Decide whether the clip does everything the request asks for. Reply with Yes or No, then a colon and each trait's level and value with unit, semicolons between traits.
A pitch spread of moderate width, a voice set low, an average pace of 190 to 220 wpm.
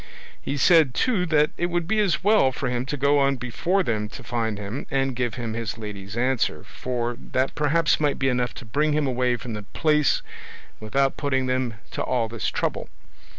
Yes: average, 4.1 semitones; low, 130 Hz; average, 200 wpm